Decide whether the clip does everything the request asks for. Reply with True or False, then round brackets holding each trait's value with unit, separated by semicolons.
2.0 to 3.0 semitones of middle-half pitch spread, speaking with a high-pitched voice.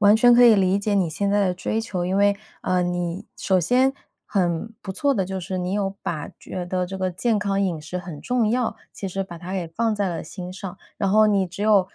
True (2.5 semitones; 195 Hz)